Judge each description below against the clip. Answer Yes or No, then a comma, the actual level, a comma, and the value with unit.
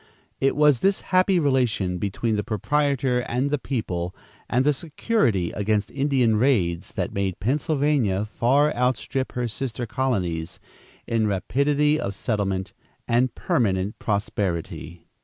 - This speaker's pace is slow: Yes, slow, 125 wpm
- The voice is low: Yes, low, 120 Hz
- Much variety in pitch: Yes, wide, 5.8 semitones